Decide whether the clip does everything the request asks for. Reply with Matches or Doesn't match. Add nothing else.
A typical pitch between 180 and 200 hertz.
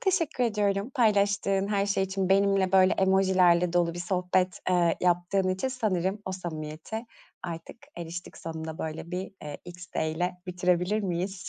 Matches